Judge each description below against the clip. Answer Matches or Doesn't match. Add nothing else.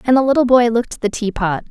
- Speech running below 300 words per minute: Doesn't match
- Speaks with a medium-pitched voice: Doesn't match